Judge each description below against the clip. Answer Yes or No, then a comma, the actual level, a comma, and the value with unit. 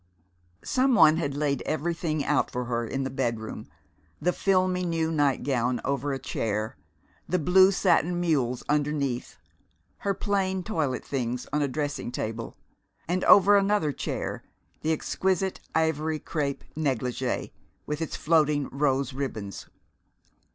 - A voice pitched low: No, medium, 150 Hz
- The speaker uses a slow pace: Yes, slow, 130 wpm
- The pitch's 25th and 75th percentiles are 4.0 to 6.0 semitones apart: Yes, average, 4.7 semitones